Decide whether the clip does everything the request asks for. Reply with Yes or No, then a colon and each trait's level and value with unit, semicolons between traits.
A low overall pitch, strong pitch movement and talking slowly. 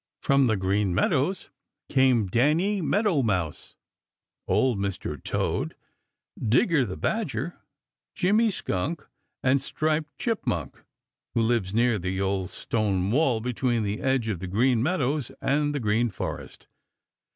Yes: low, 120 Hz; wide, 6.4 semitones; slow, 130 wpm